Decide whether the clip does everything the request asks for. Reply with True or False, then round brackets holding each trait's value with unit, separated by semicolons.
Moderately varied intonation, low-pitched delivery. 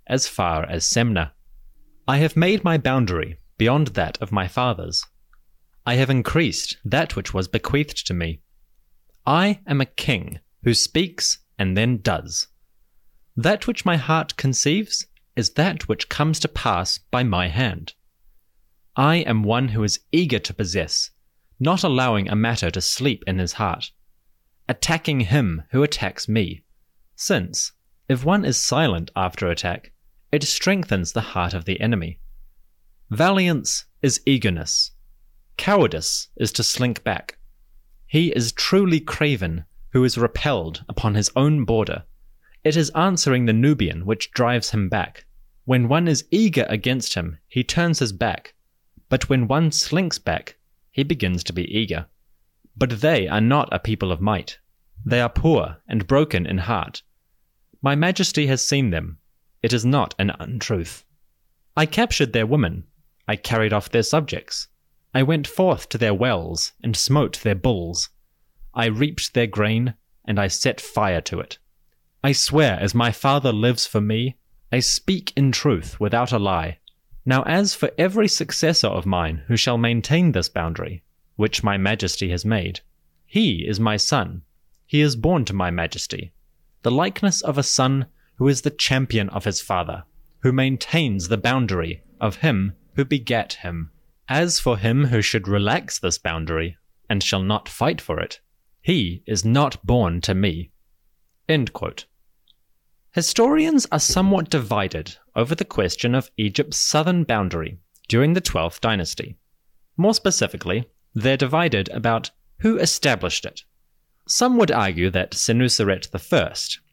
False (7.7 semitones; 110 Hz)